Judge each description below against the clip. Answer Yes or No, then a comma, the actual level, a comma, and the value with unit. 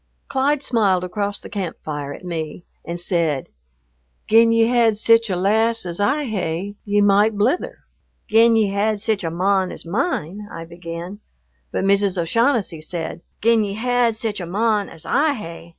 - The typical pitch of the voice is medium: No, high, 205 Hz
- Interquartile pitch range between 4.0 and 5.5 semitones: Yes, average, 4.5 semitones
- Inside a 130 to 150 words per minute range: No, average, 175 wpm